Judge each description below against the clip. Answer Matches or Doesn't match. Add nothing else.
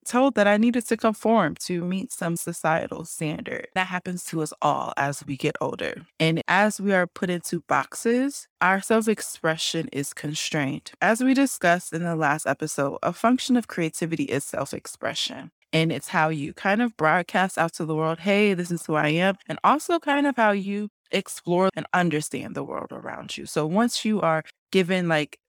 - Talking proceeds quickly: Doesn't match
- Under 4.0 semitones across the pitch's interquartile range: Doesn't match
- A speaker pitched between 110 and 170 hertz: Doesn't match